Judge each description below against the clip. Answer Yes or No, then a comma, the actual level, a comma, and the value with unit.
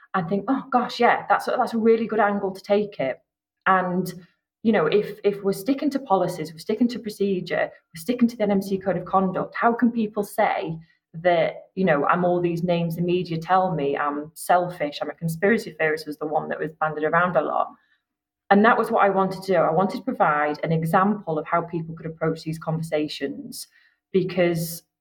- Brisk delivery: Yes, fast, 210 wpm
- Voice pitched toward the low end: No, high, 190 Hz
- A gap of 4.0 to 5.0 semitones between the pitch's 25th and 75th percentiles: Yes, average, 4.4 semitones